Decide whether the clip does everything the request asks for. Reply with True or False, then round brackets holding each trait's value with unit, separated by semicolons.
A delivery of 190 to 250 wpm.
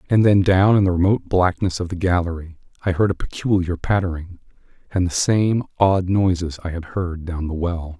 True (195 wpm)